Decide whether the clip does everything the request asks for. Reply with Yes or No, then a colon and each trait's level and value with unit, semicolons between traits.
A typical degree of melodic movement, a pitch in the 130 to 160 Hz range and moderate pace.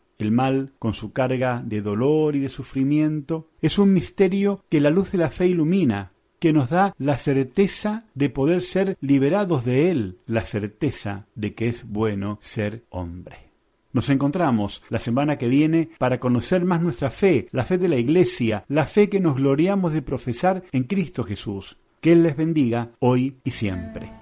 No: wide, 6.5 semitones; medium, 140 Hz; average, 180 wpm